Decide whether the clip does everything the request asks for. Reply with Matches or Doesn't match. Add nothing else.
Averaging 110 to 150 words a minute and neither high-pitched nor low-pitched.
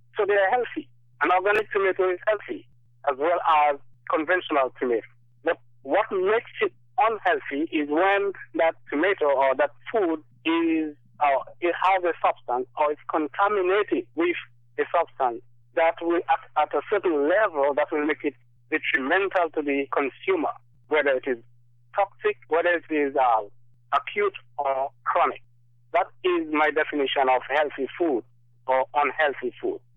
Matches